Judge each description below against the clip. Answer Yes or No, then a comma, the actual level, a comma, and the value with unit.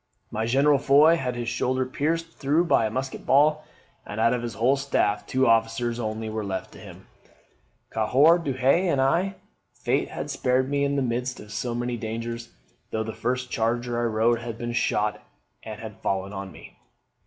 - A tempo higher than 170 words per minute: Yes, average, 190 wpm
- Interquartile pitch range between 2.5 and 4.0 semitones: Yes, average, 3.4 semitones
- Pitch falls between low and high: No, low, 120 Hz